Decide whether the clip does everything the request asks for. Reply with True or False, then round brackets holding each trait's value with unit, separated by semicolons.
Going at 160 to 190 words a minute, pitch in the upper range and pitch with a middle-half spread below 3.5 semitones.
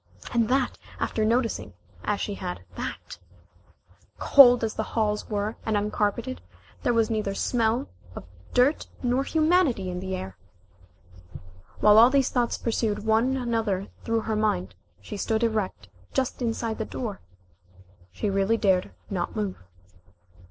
False (140 wpm; 220 Hz; 2.9 semitones)